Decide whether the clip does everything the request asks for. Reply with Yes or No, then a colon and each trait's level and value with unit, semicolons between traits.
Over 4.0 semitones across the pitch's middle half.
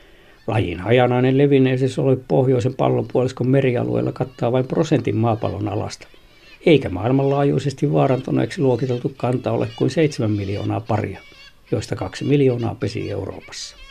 Yes: average, 4.4 semitones